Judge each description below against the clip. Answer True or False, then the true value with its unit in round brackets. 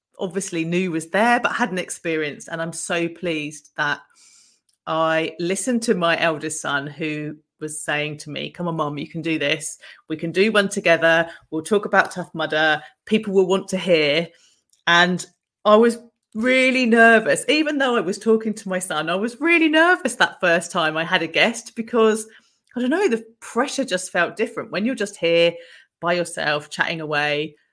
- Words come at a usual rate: True (190 wpm)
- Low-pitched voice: False (175 Hz)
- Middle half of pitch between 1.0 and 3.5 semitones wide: False (5.5 semitones)